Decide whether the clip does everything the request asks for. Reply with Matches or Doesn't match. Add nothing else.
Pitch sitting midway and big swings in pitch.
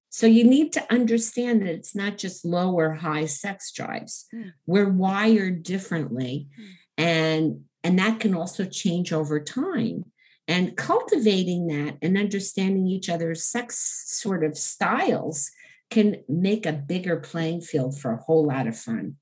Doesn't match